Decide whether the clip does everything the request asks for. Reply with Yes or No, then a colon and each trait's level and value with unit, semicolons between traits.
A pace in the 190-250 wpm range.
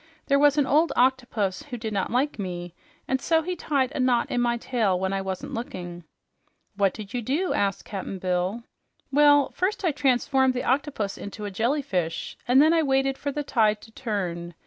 Yes: average, 195 wpm